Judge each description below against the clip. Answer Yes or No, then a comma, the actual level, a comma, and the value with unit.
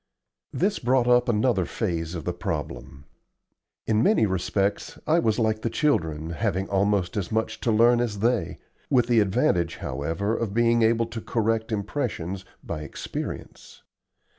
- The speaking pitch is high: No, low, 110 Hz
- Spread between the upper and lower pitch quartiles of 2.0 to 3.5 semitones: No, average, 3.9 semitones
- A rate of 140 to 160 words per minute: Yes, average, 150 wpm